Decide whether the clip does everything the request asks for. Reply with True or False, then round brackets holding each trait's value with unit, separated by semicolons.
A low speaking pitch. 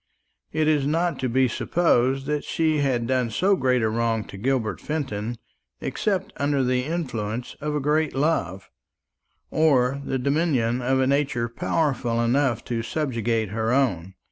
True (130 Hz)